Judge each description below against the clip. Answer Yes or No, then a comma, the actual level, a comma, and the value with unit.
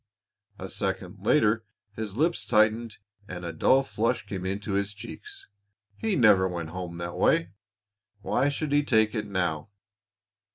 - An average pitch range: Yes, average, 4.2 semitones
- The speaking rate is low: No, average, 150 wpm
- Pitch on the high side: No, low, 105 Hz